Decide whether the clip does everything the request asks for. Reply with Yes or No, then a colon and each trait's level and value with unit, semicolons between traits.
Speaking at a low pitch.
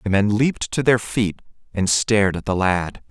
Yes: low, 105 Hz